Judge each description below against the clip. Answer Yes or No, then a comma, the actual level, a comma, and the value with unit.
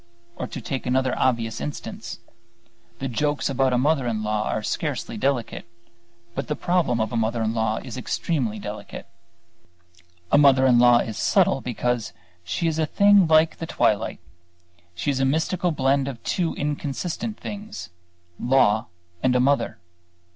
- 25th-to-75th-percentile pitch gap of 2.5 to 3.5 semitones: No, average, 4.4 semitones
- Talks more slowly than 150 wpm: No, average, 160 wpm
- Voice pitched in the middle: No, low, 130 Hz